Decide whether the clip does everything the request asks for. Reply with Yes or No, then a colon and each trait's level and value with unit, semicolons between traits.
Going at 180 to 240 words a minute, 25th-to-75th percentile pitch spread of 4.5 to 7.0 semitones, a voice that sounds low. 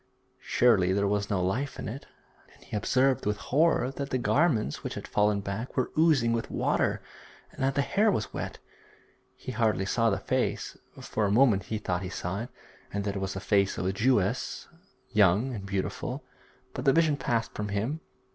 Yes: average, 195 wpm; average, 4.9 semitones; low, 110 Hz